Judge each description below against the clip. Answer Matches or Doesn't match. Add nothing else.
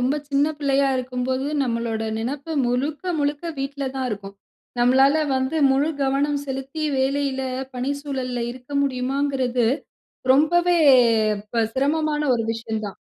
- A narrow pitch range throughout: Matches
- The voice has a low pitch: Doesn't match